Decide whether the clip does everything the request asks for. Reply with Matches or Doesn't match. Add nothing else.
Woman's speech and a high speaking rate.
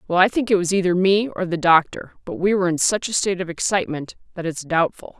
Matches